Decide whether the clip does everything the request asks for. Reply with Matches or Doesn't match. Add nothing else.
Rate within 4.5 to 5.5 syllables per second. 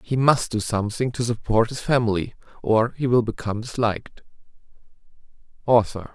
Doesn't match